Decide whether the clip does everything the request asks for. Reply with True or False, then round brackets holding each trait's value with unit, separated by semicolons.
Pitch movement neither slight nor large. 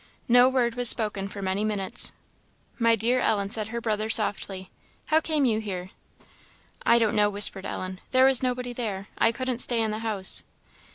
True (3.3 semitones)